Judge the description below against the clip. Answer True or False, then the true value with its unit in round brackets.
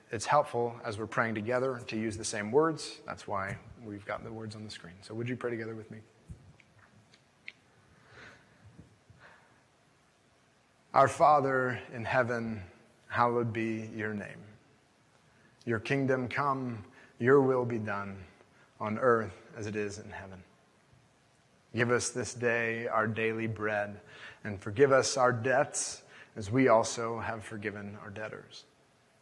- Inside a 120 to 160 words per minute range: True (140 wpm)